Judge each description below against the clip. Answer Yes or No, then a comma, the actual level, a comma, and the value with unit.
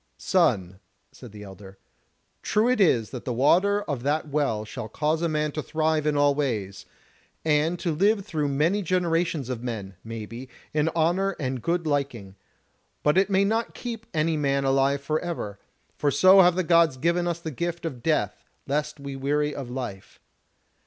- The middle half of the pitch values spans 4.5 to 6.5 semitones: Yes, average, 4.9 semitones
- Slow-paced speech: No, average, 180 wpm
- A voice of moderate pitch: Yes, medium, 150 Hz